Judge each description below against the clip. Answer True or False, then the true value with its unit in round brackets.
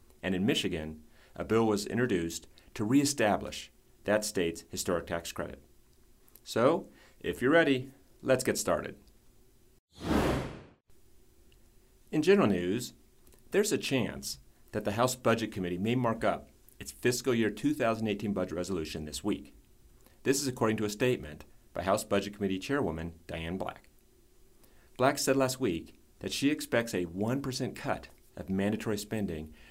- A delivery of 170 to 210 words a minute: False (140 wpm)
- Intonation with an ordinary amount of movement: False (5.7 semitones)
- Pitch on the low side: True (105 Hz)